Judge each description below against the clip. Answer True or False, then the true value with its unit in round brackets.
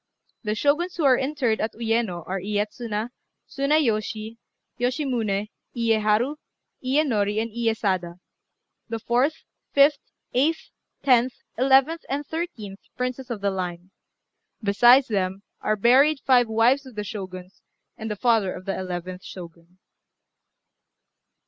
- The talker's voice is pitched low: False (225 Hz)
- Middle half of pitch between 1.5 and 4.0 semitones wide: False (4.7 semitones)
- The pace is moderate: False (120 wpm)